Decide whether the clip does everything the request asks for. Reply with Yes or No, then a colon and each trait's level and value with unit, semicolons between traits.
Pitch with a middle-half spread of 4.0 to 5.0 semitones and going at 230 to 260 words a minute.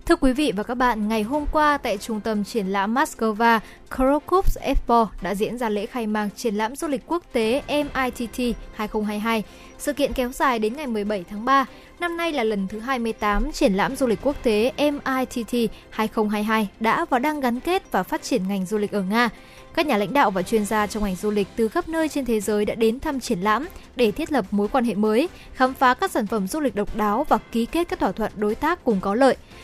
Yes: average, 4.5 semitones; average, 235 wpm